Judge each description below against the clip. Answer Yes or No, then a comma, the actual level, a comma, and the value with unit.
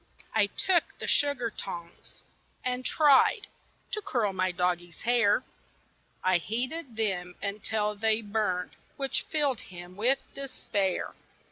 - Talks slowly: Yes, slow, 120 wpm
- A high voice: Yes, high, 215 Hz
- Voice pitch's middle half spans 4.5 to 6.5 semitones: Yes, wide, 5.6 semitones